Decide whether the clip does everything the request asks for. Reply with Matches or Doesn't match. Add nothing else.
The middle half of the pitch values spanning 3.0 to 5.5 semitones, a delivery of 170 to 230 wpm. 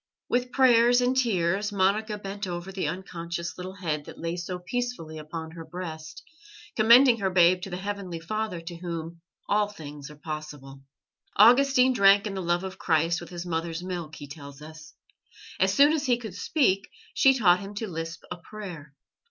Matches